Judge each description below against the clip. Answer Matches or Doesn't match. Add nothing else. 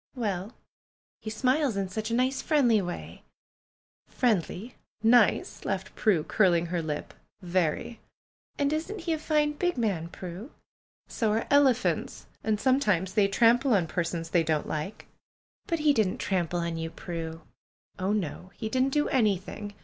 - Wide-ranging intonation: Matches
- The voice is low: Doesn't match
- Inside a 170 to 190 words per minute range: Doesn't match